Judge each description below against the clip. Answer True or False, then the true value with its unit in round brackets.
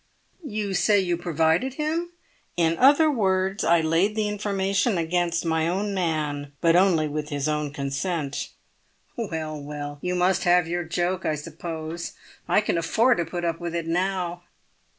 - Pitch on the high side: False (175 Hz)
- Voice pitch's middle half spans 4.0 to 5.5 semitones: False (3.3 semitones)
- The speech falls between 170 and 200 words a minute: False (160 wpm)